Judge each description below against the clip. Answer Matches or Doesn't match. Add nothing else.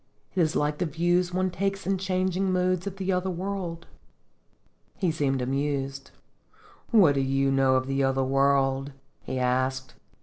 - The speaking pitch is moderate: Matches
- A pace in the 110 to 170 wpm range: Matches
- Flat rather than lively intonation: Doesn't match